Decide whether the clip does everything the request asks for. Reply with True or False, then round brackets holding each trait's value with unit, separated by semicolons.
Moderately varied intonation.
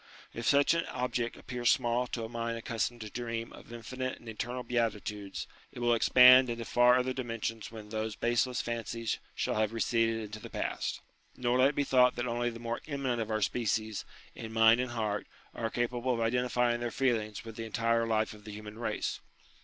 False (1.6 semitones)